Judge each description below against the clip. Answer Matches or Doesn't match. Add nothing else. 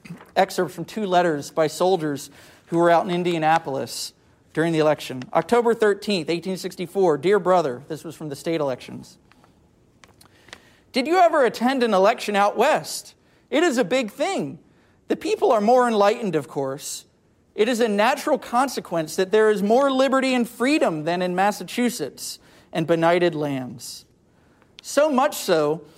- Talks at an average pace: Matches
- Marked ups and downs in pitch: Matches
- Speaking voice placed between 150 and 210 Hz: Matches